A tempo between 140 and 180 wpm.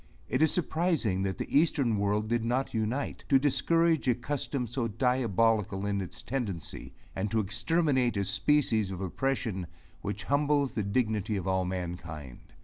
Yes: average, 155 wpm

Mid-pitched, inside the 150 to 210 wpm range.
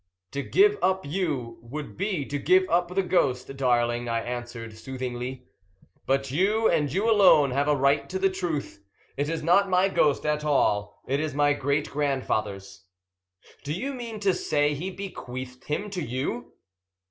Yes: medium, 145 Hz; average, 170 wpm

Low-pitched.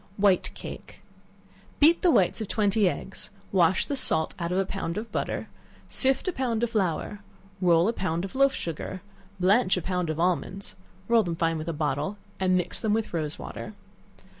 No: high, 190 Hz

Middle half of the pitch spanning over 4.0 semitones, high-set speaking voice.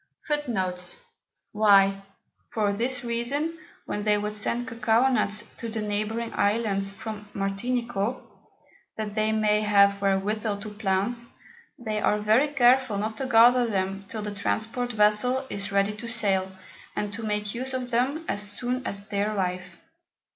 No: average, 2.8 semitones; high, 215 Hz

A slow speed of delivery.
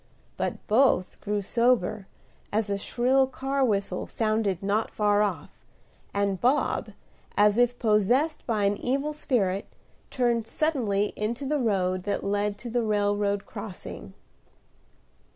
Yes: slow, 130 wpm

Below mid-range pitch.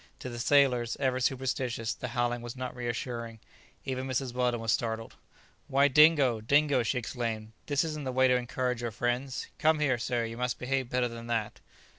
Yes: low, 125 Hz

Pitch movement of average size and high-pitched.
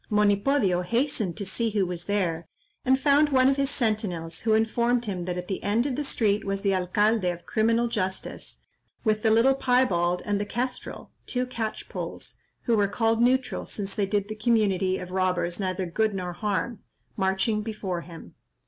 Yes: average, 3.9 semitones; high, 210 Hz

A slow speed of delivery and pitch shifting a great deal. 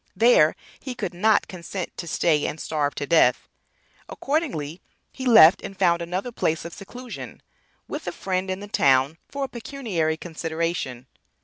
No: average, 155 wpm; wide, 5.7 semitones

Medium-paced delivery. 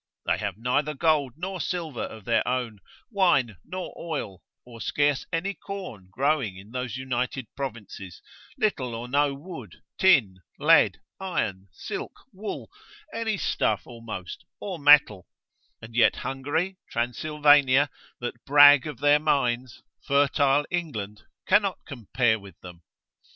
No: slow, 130 wpm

